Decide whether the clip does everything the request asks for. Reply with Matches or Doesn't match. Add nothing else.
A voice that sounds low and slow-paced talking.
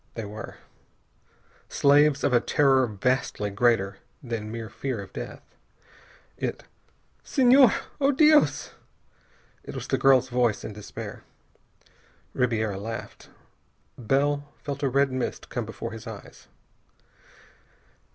Matches